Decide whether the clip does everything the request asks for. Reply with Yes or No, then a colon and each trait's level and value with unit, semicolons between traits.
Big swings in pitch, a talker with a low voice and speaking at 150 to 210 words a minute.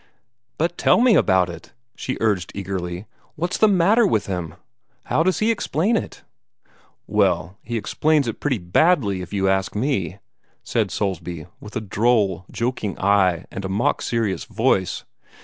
Yes: wide, 6.8 semitones; low, 105 Hz; average, 155 wpm